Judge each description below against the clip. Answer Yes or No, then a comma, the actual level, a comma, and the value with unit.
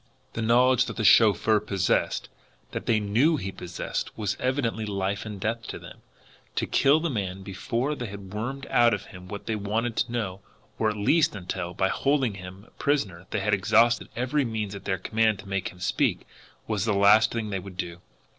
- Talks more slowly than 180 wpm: No, average, 200 wpm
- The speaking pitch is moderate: No, low, 105 Hz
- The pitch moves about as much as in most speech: Yes, average, 3.3 semitones